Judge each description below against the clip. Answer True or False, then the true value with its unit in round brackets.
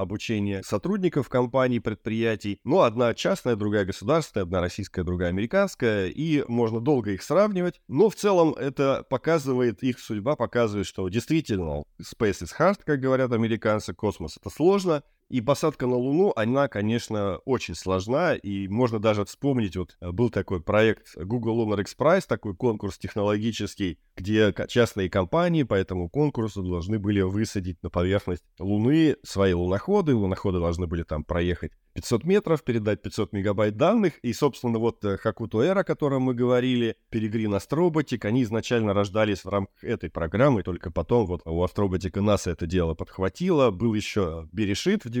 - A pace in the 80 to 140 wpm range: False (155 wpm)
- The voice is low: True (110 Hz)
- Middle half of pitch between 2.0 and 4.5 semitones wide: False (5.1 semitones)